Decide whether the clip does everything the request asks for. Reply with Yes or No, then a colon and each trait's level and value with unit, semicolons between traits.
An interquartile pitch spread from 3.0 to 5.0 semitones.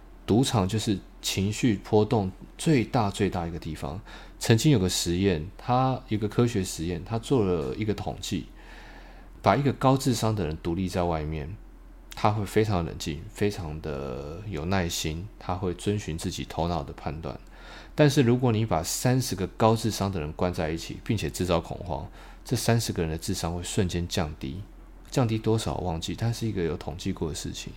Yes: average, 4.4 semitones